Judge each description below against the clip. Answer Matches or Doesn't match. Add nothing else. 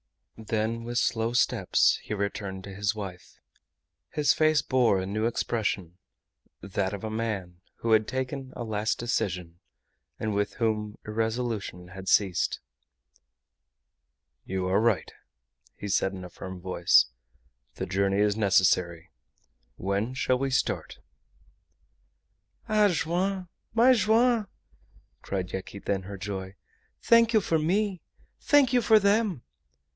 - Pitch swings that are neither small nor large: Doesn't match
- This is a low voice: Matches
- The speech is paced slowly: Matches